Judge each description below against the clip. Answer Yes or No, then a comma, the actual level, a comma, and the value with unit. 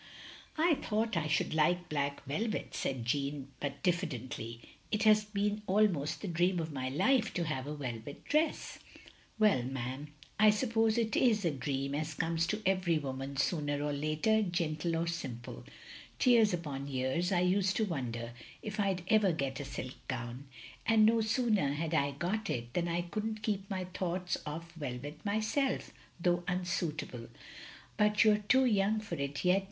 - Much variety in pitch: Yes, wide, 6.8 semitones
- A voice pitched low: No, medium, 170 Hz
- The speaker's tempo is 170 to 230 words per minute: Yes, average, 180 wpm